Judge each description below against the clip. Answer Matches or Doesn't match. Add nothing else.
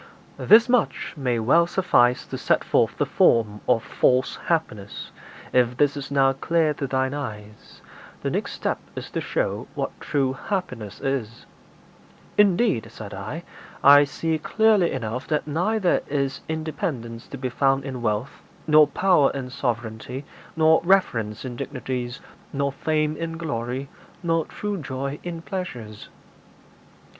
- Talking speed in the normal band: Matches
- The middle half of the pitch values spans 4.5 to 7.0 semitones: Matches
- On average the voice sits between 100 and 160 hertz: Matches